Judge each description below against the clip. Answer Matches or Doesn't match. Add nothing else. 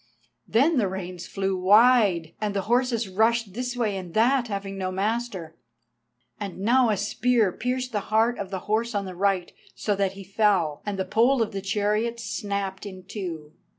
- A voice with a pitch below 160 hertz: Doesn't match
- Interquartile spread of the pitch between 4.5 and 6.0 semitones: Doesn't match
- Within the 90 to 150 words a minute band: Doesn't match